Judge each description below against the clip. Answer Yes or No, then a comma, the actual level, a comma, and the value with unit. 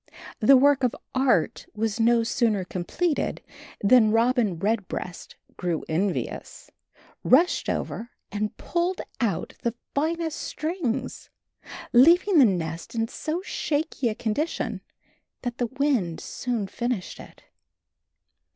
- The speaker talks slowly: Yes, slow, 115 wpm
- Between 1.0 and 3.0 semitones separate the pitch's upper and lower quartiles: No, wide, 5.5 semitones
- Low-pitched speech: No, high, 240 Hz